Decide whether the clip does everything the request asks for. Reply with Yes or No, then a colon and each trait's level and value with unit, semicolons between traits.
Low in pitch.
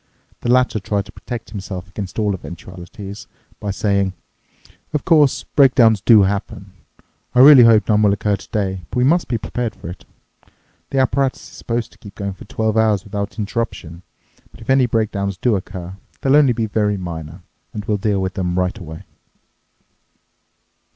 Yes: low, 105 Hz